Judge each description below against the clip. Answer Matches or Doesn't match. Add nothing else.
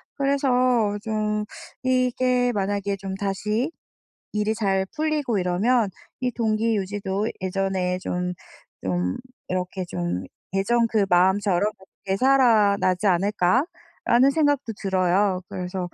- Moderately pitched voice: Doesn't match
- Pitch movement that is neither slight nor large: Matches